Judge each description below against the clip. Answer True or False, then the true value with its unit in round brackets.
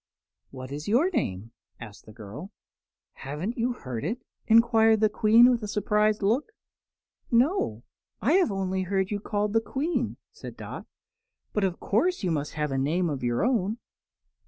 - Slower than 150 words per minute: False (165 wpm)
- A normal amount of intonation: False (7.7 semitones)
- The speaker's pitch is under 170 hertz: False (205 Hz)